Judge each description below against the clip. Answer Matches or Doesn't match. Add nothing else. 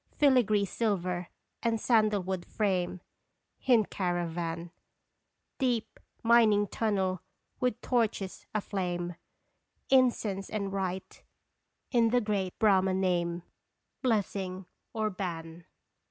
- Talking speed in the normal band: Doesn't match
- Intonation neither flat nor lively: Matches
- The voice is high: Matches